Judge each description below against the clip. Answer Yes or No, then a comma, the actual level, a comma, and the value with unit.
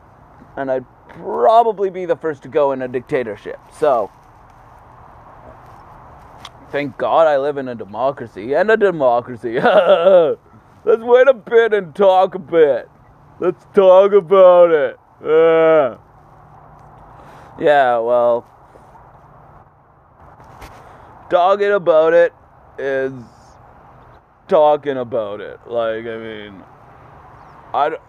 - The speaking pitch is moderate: Yes, medium, 160 Hz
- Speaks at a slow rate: Yes, slow, 105 wpm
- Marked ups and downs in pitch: Yes, wide, 7.6 semitones